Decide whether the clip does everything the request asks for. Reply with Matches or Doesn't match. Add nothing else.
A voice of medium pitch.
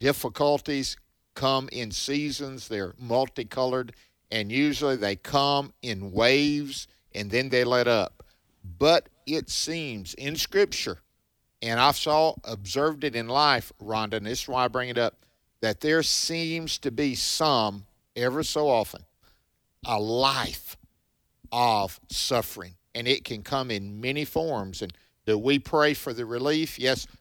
Doesn't match